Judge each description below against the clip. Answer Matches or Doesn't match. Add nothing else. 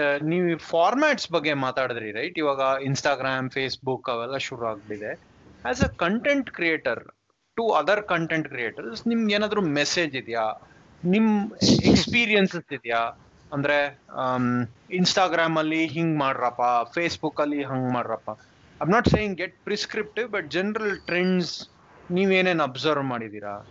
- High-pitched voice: Doesn't match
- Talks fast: Matches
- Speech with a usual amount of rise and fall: Doesn't match